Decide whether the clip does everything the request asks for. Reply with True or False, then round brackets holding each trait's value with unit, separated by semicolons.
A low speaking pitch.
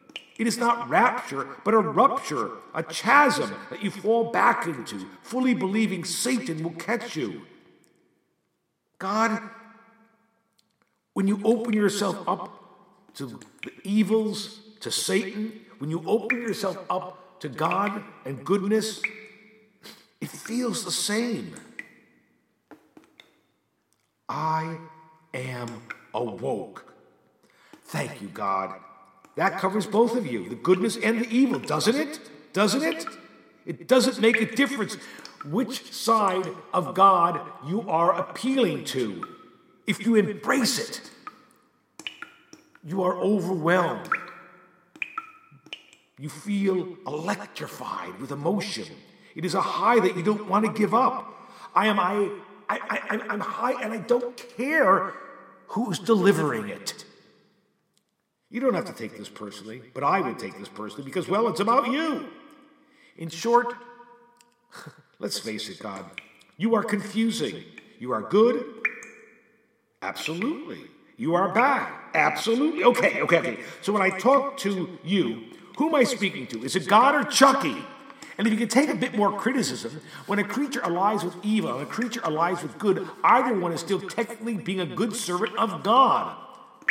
False (220 Hz)